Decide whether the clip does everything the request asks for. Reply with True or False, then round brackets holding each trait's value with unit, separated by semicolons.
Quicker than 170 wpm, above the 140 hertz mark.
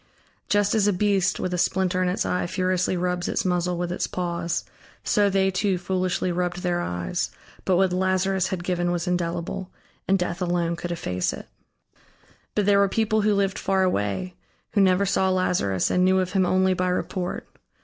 True (190 wpm; 185 Hz)